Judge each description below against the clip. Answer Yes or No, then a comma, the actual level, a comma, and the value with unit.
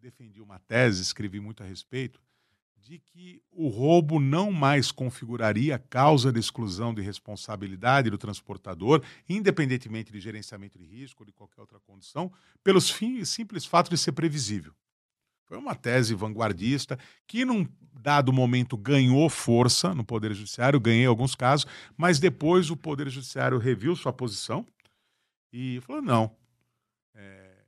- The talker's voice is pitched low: Yes, low, 125 Hz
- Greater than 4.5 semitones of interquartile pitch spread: Yes, wide, 5.6 semitones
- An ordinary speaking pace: Yes, average, 145 wpm